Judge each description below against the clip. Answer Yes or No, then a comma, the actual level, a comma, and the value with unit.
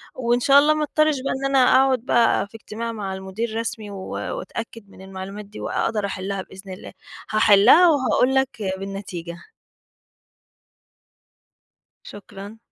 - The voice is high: Yes, high, 215 Hz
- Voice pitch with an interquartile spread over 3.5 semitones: Yes, average, 4.6 semitones